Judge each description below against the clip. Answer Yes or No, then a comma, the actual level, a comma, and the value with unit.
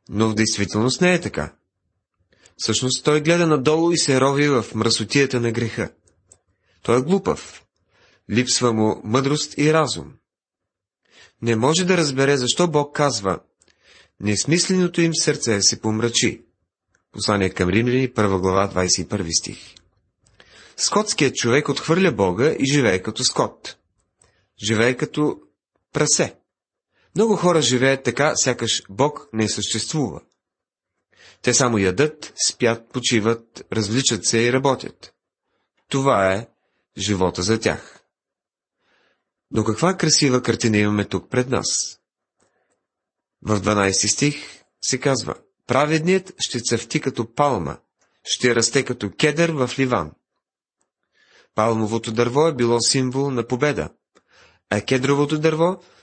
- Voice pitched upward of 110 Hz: Yes, low, 120 Hz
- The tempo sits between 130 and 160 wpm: No, average, 120 wpm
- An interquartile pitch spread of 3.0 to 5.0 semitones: No, wide, 5.5 semitones